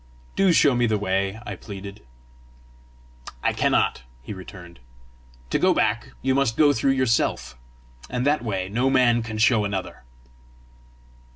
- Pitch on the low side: Yes, low, 115 Hz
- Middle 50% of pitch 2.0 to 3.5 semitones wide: No, average, 4.7 semitones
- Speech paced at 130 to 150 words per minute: Yes, average, 145 wpm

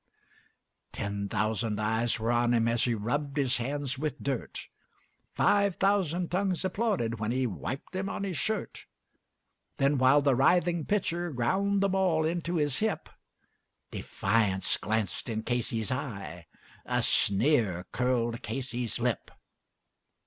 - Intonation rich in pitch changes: Yes, wide, 7.2 semitones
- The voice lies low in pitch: Yes, low, 130 Hz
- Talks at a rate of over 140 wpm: No, slow, 135 wpm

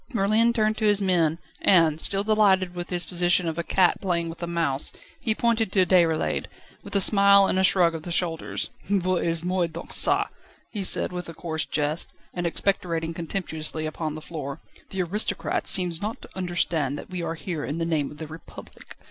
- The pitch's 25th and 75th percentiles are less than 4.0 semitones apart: Yes, average, 2.9 semitones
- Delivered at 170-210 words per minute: Yes, average, 200 wpm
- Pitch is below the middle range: No, medium, 175 Hz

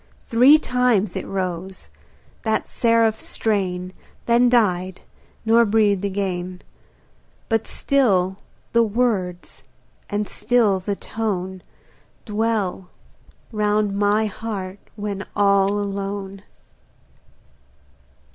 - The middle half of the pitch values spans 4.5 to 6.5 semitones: No, average, 2.9 semitones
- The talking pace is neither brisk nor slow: No, slow, 90 wpm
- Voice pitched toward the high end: Yes, high, 205 Hz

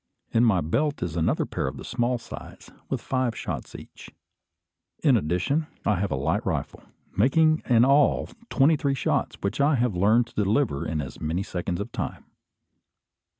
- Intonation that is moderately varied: No, wide, 7.4 semitones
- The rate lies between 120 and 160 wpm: No, average, 175 wpm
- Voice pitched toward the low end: Yes, low, 115 Hz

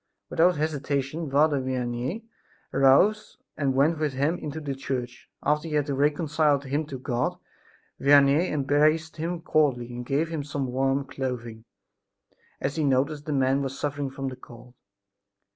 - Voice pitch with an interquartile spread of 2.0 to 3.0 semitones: Yes, narrow, 2.5 semitones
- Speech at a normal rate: Yes, average, 150 wpm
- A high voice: No, medium, 140 Hz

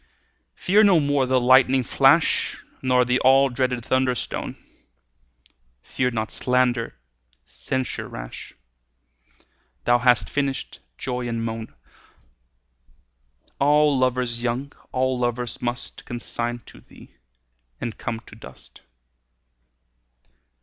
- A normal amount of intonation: No, narrow, 1.5 semitones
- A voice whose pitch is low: Yes, low, 125 Hz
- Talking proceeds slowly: Yes, slow, 105 wpm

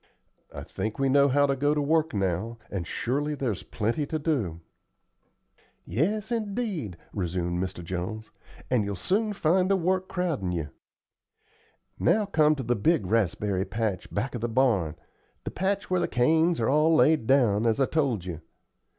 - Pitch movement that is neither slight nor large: No, wide, 8.0 semitones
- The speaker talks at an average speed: Yes, average, 170 wpm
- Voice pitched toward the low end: Yes, low, 130 Hz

